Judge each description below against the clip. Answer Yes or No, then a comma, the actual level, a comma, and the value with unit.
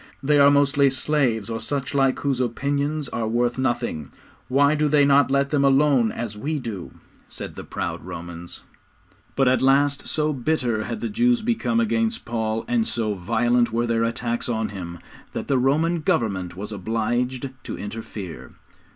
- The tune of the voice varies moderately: Yes, average, 4.2 semitones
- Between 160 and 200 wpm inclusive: Yes, average, 170 wpm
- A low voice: Yes, low, 130 Hz